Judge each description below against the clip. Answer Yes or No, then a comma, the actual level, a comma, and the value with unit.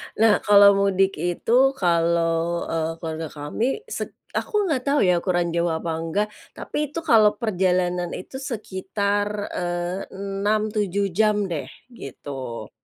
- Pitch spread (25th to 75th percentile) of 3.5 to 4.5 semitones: Yes, average, 3.8 semitones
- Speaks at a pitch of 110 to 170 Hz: No, high, 195 Hz